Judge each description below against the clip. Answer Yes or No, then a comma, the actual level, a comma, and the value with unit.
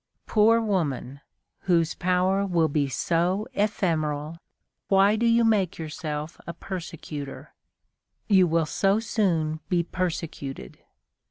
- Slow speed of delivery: Yes, slow, 110 wpm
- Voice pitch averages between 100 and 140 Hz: No, medium, 175 Hz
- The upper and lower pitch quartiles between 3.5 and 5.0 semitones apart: Yes, average, 4.1 semitones